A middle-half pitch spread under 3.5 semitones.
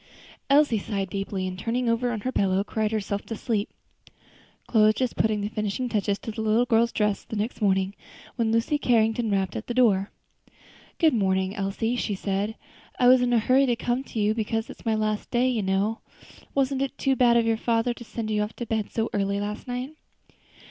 Yes: average, 2.9 semitones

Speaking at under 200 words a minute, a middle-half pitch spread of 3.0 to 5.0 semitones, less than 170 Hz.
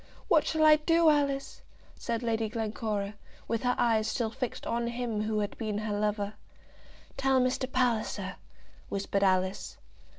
No: average, 145 wpm; average, 3.4 semitones; high, 230 Hz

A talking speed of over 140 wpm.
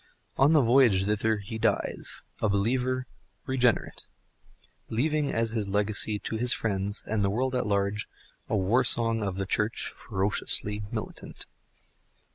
No: slow, 135 wpm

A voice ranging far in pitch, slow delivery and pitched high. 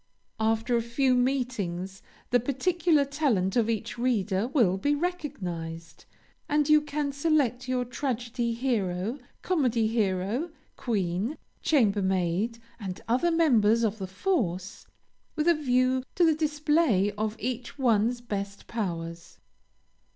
Yes: wide, 5.9 semitones; slow, 120 wpm; high, 235 Hz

